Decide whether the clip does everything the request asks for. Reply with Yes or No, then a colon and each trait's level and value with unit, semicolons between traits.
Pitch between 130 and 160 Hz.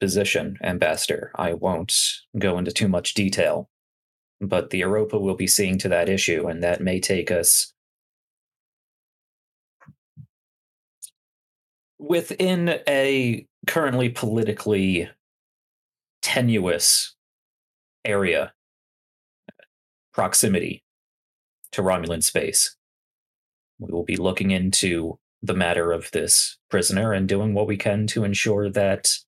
No: low, 100 Hz